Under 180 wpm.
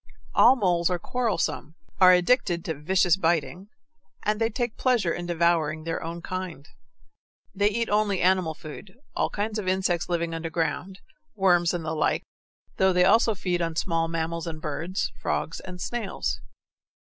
Yes: average, 160 wpm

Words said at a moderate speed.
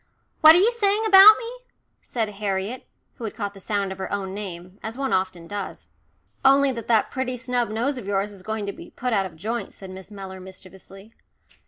No: fast, 210 wpm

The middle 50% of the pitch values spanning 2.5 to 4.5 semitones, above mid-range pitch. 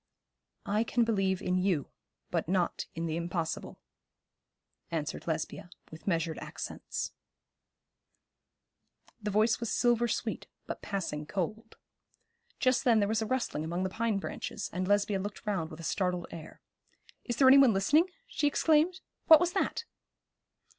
No: wide, 5.4 semitones; high, 200 Hz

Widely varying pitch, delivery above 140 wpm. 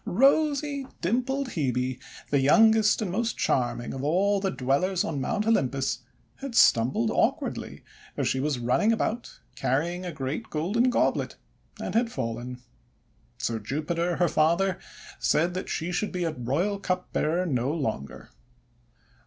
No: wide, 7.9 semitones; slow, 135 wpm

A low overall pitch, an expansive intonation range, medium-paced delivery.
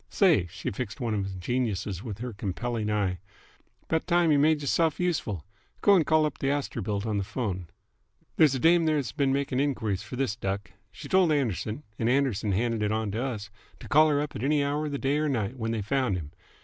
No: low, 125 Hz; wide, 5.8 semitones; fast, 225 wpm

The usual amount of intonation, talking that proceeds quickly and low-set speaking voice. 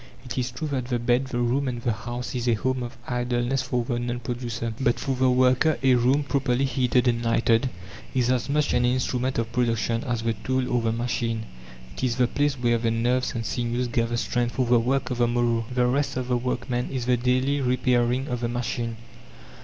No: narrow, 1.4 semitones; fast, 220 wpm; low, 125 Hz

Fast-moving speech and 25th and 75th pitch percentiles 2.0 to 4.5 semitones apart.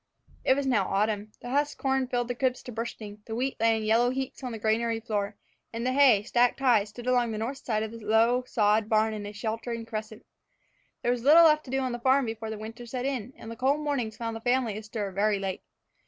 Yes: fast, 245 wpm; average, 2.8 semitones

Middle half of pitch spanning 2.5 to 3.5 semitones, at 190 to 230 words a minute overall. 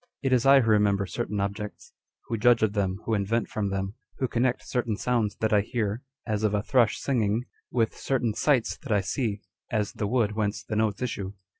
Yes: average, 2.8 semitones; average, 200 wpm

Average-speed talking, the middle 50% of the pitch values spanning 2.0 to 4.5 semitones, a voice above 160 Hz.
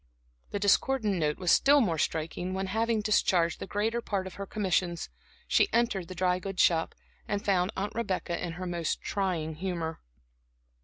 Yes: average, 170 wpm; average, 3.1 semitones; high, 190 Hz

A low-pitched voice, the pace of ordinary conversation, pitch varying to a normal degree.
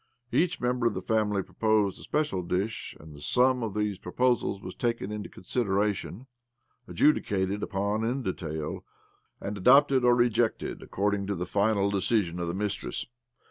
Yes: low, 105 Hz; average, 155 wpm; average, 3.7 semitones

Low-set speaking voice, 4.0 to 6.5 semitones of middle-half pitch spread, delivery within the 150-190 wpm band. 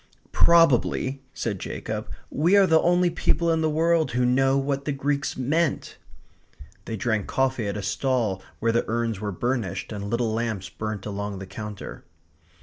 Yes: low, 125 Hz; wide, 5.5 semitones; average, 165 wpm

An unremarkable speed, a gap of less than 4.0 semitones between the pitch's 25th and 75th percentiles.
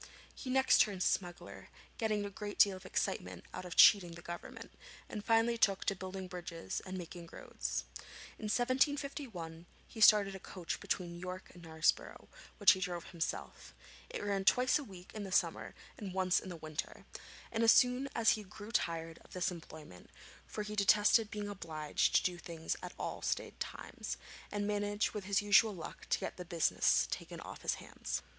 Yes: average, 180 wpm; average, 3.3 semitones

